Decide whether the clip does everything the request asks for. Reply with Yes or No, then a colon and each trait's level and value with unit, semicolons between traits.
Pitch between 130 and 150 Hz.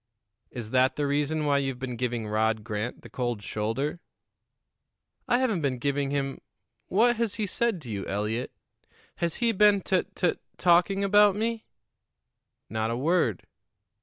Yes: medium, 140 Hz